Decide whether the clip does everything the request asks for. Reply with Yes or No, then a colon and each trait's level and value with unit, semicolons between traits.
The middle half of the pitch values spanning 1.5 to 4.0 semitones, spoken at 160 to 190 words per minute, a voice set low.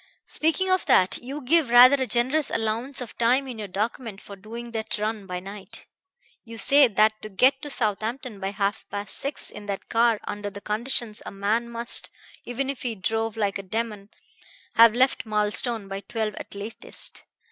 No: average, 3.2 semitones; average, 185 wpm; high, 225 Hz